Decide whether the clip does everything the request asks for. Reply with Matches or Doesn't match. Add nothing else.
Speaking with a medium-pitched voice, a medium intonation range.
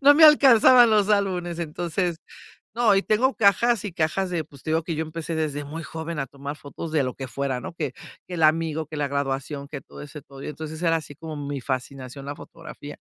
Matches